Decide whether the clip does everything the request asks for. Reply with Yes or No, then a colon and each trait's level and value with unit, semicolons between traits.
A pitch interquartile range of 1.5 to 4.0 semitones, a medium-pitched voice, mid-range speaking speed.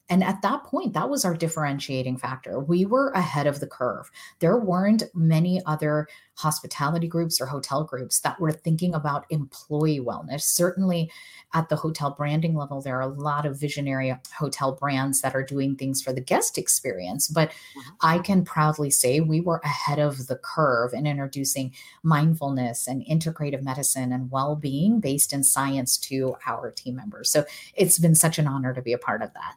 Yes: average, 3.3 semitones; medium, 150 Hz; average, 185 wpm